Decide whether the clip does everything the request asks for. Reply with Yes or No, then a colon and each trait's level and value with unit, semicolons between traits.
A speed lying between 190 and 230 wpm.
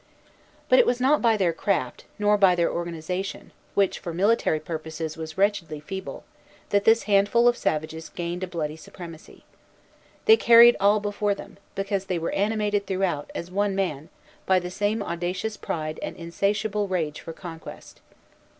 No: average, 160 wpm